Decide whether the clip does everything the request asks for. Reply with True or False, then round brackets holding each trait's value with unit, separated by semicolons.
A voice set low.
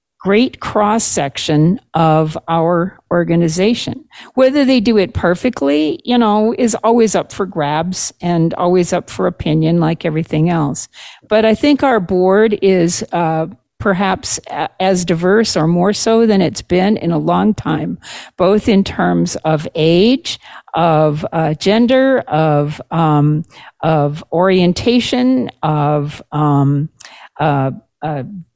False (175 Hz)